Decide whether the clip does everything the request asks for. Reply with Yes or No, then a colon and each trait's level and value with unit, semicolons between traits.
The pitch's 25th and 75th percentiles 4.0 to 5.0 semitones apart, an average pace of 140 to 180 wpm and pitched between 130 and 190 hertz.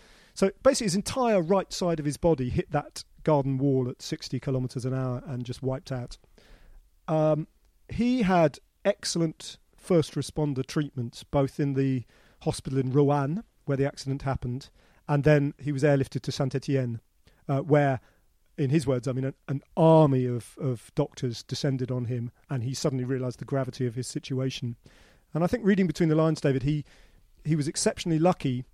No: average, 3.5 semitones; average, 175 wpm; medium, 140 Hz